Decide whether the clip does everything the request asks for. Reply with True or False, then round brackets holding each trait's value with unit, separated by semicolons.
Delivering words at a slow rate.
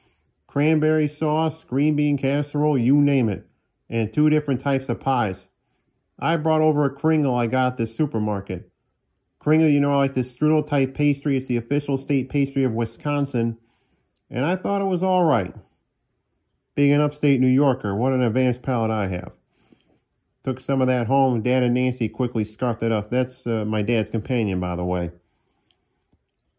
False (175 wpm)